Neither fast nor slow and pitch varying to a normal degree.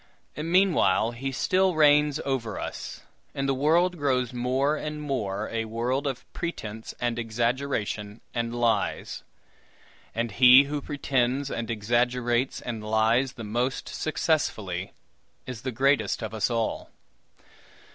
No: slow, 125 wpm; average, 3.6 semitones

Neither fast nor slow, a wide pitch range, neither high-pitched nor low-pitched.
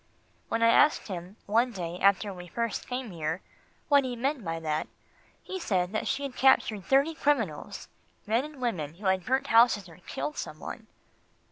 No: average, 180 wpm; wide, 6.6 semitones; high, 220 Hz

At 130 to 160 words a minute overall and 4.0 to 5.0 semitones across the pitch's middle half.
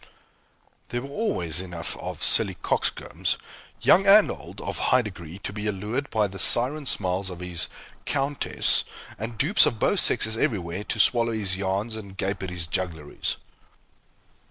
Yes: average, 155 wpm; average, 4.7 semitones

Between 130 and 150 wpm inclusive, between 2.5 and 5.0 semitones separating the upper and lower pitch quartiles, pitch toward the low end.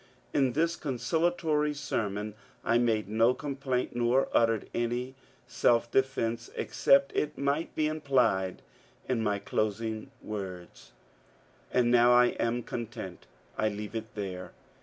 Yes: slow, 135 wpm; average, 3.9 semitones; low, 120 Hz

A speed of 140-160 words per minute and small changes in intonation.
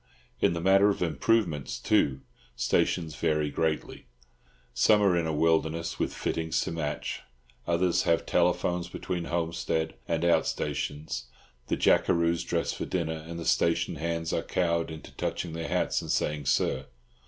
Yes: average, 155 wpm; narrow, 1.4 semitones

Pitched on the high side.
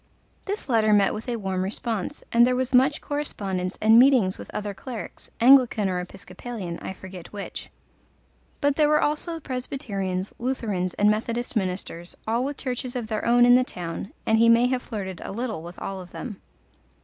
Yes: high, 225 Hz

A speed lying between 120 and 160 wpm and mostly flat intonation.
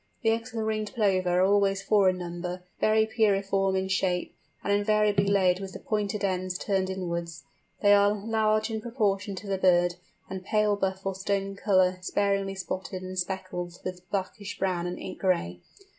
No: average, 180 wpm; narrow, 1.8 semitones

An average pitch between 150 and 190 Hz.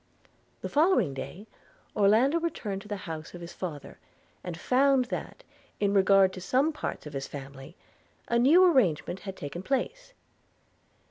No: high, 200 Hz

